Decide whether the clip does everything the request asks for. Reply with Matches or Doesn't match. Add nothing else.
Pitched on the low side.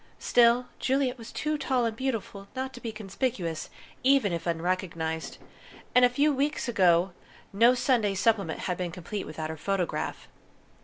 Doesn't match